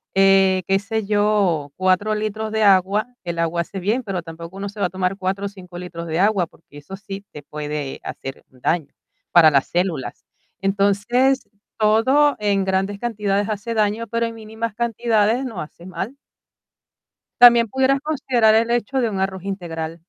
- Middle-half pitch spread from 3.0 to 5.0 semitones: Yes, average, 3.6 semitones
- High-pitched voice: Yes, high, 200 Hz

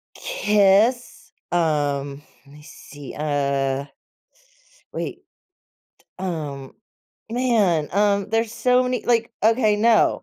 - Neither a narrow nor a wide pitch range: No, wide, 7.8 semitones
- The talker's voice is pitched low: No, high, 195 Hz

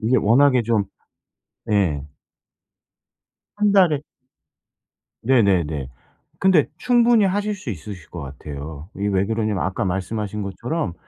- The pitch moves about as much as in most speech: No, wide, 8.0 semitones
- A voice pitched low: Yes, low, 105 Hz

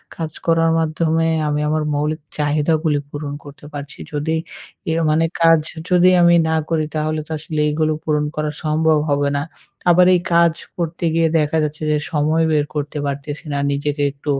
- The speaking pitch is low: No, medium, 155 Hz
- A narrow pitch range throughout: Yes, narrow, 1.7 semitones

